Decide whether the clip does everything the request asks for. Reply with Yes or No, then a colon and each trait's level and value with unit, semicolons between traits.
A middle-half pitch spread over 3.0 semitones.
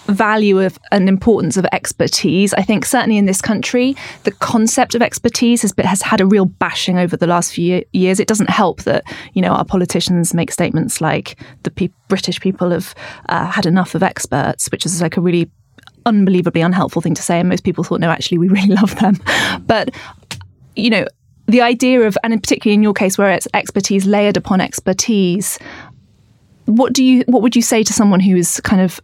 Yes: average, 3.7 semitones